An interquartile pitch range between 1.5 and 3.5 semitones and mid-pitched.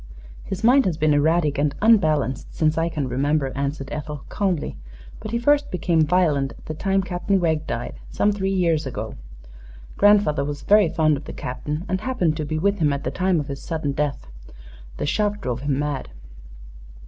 No: average, 4.8 semitones; medium, 155 Hz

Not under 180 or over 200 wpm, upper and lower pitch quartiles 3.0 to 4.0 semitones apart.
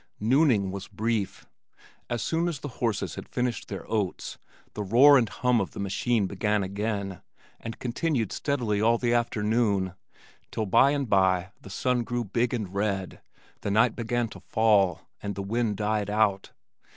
No: average, 165 wpm; average, 3.3 semitones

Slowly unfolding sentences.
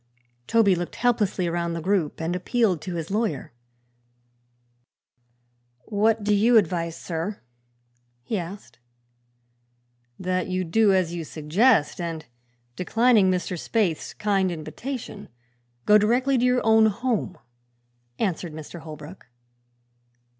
Yes: slow, 115 wpm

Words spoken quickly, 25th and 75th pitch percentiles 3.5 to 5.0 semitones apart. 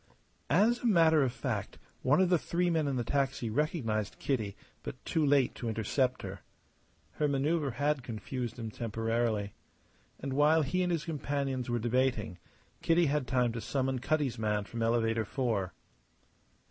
No: average, 160 wpm; average, 4.7 semitones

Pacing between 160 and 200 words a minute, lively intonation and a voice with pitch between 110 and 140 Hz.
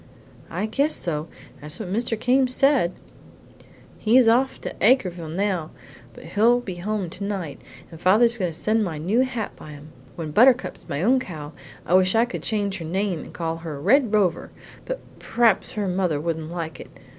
No: average, 180 wpm; wide, 5.8 semitones; high, 195 Hz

